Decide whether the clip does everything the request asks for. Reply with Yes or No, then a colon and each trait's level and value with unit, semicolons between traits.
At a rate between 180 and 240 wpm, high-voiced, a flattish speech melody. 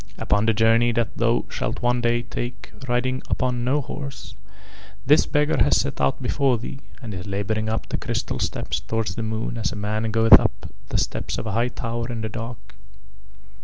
No: average, 195 wpm; low, 115 Hz; narrow, 2.0 semitones